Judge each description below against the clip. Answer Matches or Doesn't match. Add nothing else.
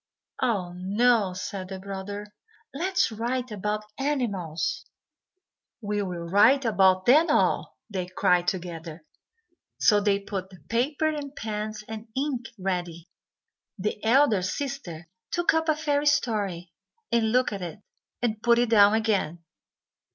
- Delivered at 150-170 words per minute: Doesn't match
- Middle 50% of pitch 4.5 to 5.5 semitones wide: Matches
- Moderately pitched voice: Doesn't match